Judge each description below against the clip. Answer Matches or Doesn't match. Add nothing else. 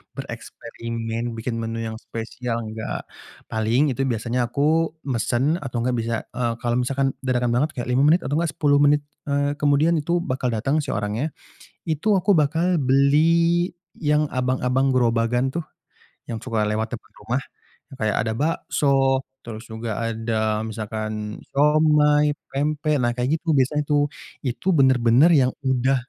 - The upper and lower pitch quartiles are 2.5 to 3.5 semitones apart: Doesn't match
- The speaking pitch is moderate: Doesn't match